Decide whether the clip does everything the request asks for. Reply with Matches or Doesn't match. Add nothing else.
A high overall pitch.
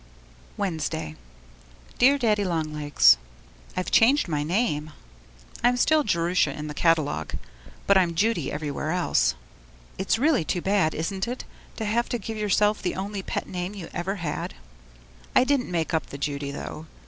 Doesn't match